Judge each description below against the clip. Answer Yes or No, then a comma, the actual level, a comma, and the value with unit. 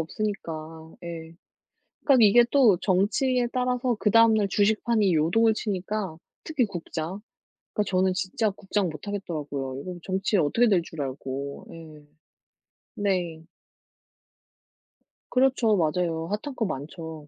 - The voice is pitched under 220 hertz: Yes, high, 190 Hz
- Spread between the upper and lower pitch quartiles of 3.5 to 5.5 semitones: Yes, average, 5.2 semitones